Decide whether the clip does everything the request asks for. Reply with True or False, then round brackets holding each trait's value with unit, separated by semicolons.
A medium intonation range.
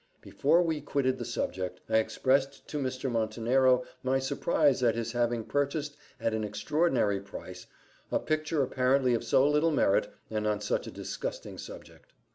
True (4.3 semitones)